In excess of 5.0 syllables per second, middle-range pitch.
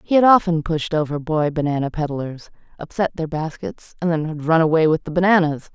Yes: 5.5 syllables/s; medium, 160 Hz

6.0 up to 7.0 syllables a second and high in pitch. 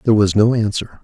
No: 6.6 syllables/s; low, 105 Hz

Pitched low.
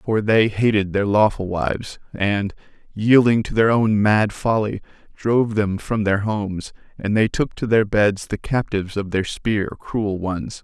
Yes: low, 105 Hz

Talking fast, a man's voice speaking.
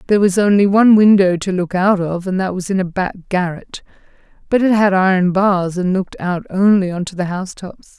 No: fast, 220 wpm; female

